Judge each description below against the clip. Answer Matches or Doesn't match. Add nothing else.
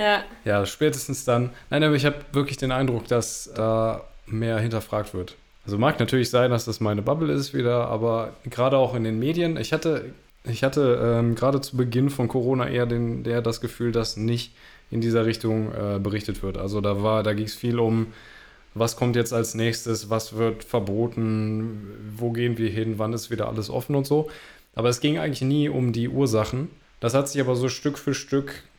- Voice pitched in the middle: Doesn't match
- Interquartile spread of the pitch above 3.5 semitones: Doesn't match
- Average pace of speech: Doesn't match